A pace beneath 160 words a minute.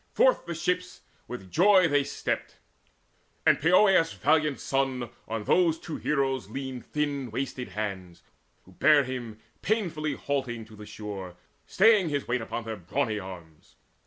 Yes: average, 145 wpm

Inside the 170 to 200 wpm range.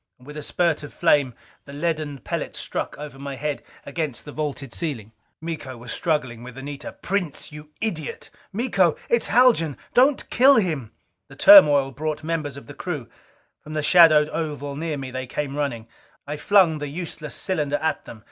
Yes: average, 175 wpm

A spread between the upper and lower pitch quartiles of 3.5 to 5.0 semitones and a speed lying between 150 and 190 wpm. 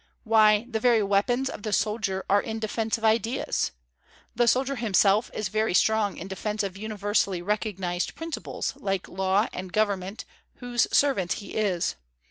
No: narrow, 2.5 semitones; average, 155 wpm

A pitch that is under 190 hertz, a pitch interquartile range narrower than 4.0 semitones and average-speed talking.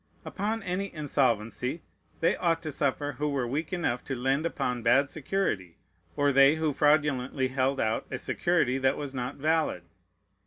Yes: medium, 140 Hz; average, 3.5 semitones; average, 160 wpm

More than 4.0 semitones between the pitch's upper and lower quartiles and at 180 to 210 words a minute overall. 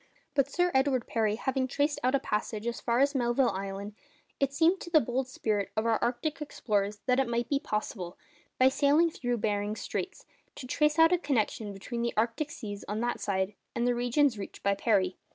Yes: average, 4.8 semitones; fast, 205 wpm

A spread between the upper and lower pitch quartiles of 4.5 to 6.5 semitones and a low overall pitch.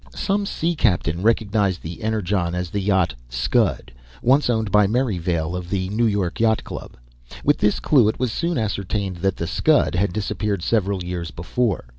No: average, 3.8 semitones; low, 100 Hz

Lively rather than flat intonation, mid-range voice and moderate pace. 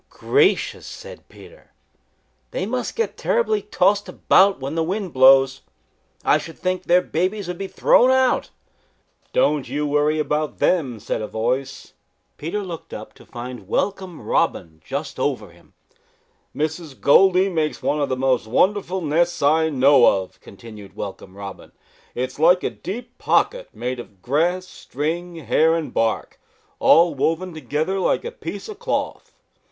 Yes: wide, 5.9 semitones; medium, 155 Hz; average, 155 wpm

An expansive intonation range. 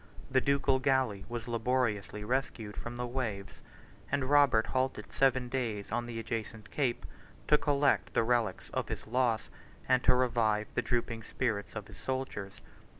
No: average, 3.1 semitones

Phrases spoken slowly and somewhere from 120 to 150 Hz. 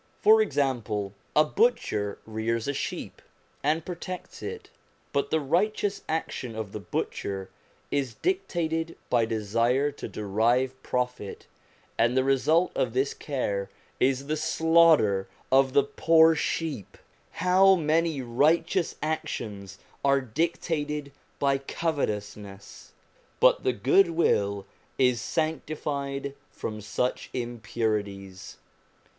Yes: slow, 110 wpm; low, 135 Hz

